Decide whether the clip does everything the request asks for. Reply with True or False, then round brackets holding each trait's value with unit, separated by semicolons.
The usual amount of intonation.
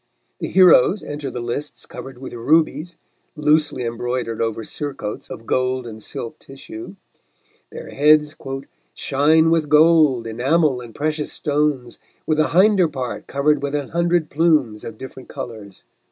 True (4.1 semitones)